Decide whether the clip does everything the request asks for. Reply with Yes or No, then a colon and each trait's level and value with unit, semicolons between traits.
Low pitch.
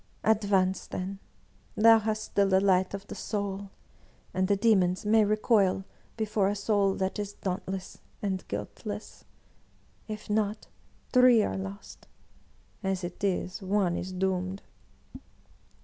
No: high, 195 Hz